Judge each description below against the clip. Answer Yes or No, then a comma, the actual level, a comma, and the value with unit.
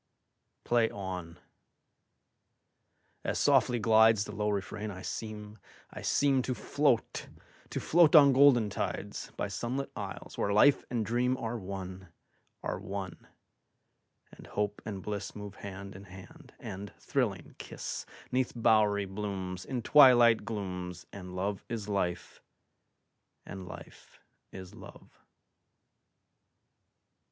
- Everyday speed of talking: No, slow, 105 wpm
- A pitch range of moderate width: Yes, average, 3.6 semitones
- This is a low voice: Yes, low, 105 Hz